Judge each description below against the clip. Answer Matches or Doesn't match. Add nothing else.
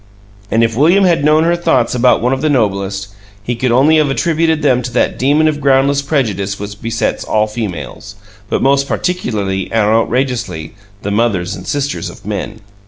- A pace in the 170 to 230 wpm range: Matches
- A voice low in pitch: Matches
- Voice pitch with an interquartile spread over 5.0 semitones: Matches